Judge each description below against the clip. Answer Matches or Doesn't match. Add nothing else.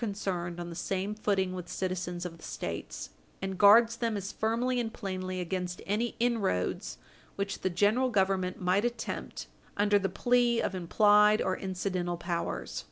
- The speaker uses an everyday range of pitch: Matches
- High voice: Matches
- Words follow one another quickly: Doesn't match